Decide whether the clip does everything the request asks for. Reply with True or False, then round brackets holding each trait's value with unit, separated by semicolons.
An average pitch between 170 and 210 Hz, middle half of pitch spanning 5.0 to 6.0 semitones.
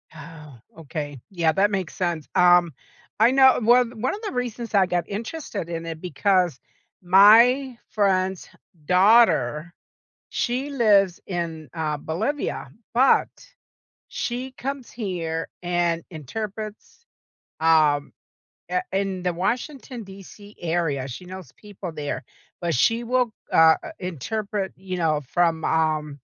True (185 Hz; 5.5 semitones)